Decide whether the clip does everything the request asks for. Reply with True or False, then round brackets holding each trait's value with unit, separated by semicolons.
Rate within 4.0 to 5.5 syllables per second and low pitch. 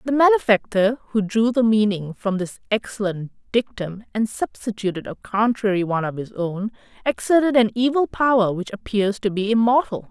False (5.2 syllables/s; 215 Hz)